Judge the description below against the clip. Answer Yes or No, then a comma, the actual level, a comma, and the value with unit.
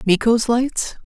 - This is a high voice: Yes, high, 235 Hz